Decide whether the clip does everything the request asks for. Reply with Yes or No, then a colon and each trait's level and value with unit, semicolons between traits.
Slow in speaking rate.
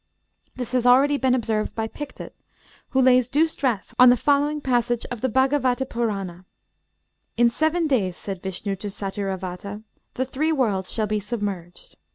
No: average, 160 wpm